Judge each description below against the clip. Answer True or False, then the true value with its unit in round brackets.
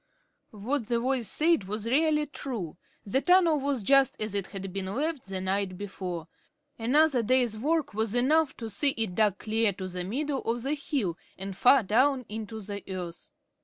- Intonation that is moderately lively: False (5.7 semitones)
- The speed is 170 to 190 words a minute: True (180 wpm)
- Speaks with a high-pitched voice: True (225 Hz)